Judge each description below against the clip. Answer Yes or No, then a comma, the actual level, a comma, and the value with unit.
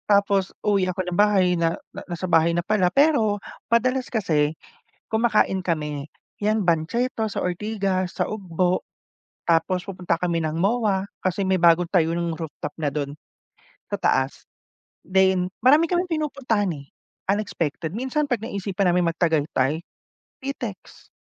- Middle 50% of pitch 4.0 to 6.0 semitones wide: Yes, average, 4.4 semitones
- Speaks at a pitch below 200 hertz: Yes, medium, 185 Hz